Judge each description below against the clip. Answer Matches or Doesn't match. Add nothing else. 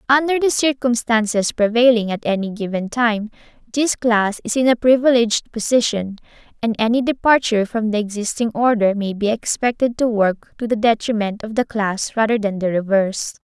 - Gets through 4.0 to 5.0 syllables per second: Doesn't match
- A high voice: Matches